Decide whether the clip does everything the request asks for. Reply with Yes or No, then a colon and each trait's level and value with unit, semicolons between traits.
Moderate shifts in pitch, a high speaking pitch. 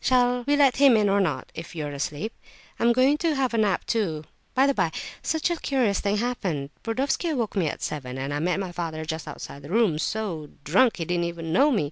No: wide, 7.7 semitones; high, 200 Hz